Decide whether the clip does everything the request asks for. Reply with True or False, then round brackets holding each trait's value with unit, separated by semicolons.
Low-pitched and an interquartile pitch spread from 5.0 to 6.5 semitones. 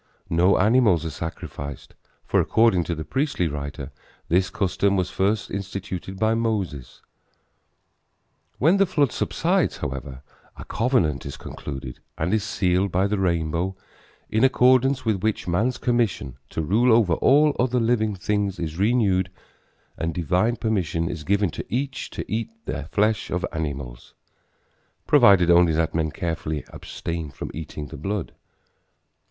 True (95 Hz; 5.4 semitones)